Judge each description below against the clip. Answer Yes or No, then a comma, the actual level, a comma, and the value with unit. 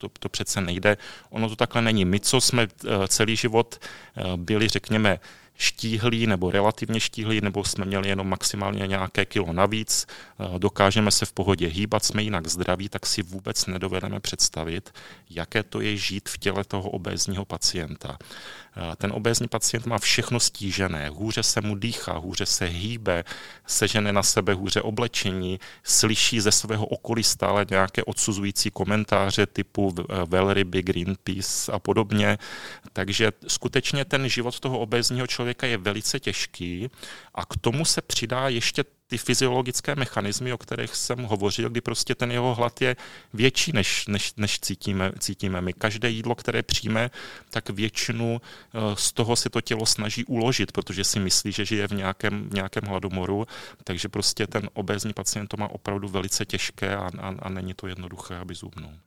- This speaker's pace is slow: No, average, 160 wpm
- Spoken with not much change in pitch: No, average, 3.1 semitones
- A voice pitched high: No, low, 105 Hz